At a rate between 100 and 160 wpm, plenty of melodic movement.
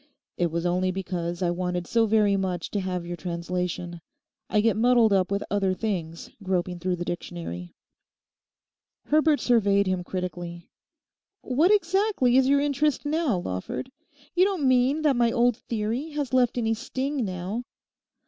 Yes: average, 155 wpm; wide, 6.3 semitones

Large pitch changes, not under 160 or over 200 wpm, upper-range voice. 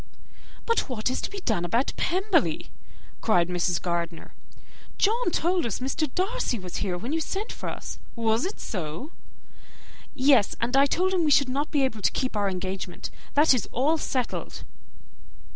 Yes: wide, 8.4 semitones; average, 170 wpm; very high, 255 Hz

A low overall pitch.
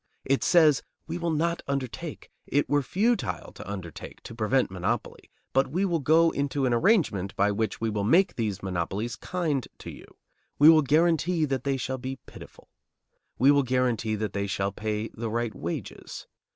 Yes: low, 130 Hz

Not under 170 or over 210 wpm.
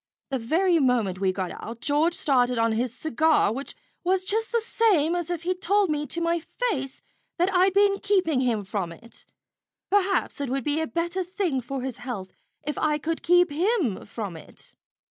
Yes: average, 190 wpm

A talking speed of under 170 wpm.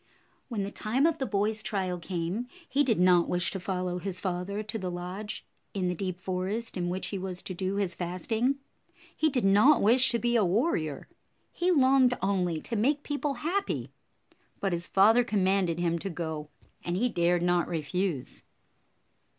No: average, 185 wpm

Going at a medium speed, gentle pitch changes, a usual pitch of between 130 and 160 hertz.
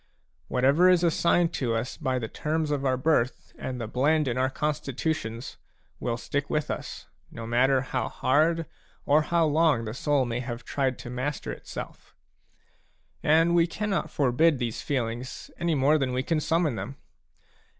No: average, 165 wpm; average, 4.1 semitones; low, 135 Hz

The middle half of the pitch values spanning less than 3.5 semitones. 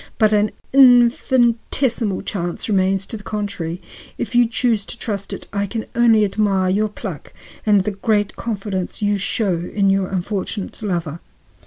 Yes: narrow, 2.6 semitones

